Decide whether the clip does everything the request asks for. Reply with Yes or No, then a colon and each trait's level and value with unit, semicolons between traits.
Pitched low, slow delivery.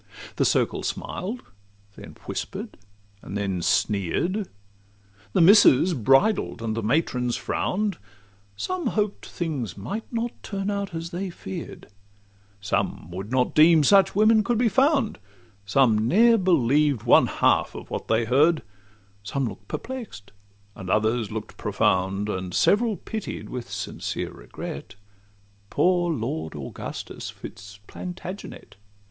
No: medium, 155 Hz; slow, 125 wpm